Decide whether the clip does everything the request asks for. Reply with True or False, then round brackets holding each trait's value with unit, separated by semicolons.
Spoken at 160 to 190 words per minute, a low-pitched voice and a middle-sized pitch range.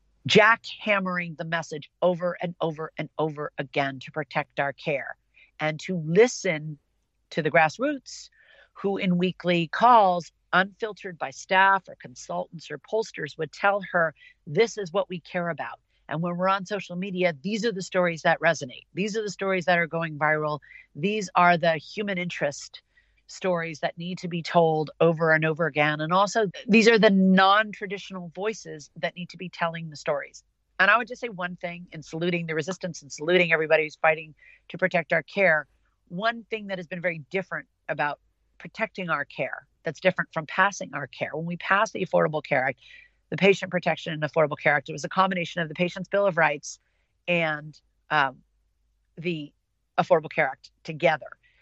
False (185 wpm; 175 Hz; 3.4 semitones)